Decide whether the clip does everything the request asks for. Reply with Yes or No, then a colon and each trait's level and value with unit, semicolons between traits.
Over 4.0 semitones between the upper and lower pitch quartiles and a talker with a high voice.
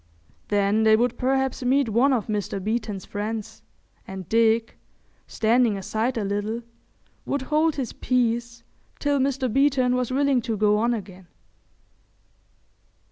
No: average, 3.3 semitones; high, 230 Hz